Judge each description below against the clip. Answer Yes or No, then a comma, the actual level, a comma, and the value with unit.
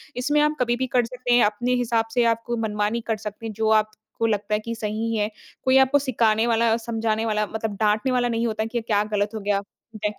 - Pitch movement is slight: Yes, narrow, 1.9 semitones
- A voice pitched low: No, high, 225 Hz